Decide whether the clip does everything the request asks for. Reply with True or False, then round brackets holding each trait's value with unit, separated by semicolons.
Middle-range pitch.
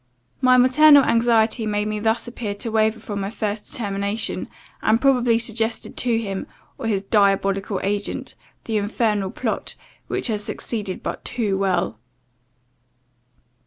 False (215 Hz)